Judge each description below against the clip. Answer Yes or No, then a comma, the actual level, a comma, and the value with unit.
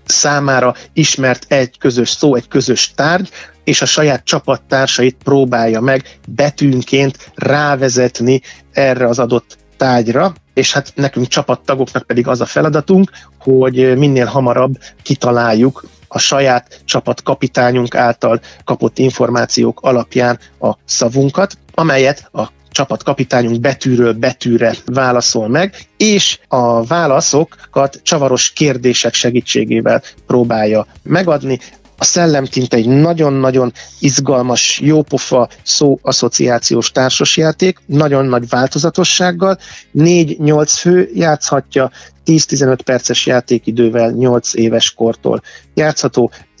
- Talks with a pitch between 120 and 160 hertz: Yes, low, 130 Hz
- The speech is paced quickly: No, slow, 100 wpm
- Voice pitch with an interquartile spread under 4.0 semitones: Yes, average, 2.9 semitones